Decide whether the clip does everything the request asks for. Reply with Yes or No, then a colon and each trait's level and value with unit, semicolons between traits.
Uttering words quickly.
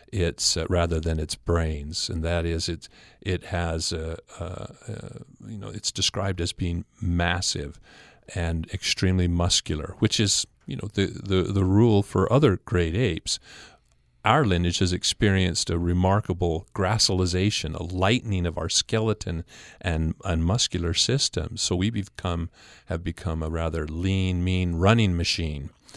No: average, 150 wpm